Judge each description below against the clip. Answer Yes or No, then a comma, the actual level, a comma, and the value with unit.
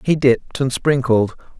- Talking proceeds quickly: No, average, 150 wpm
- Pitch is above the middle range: No, low, 130 Hz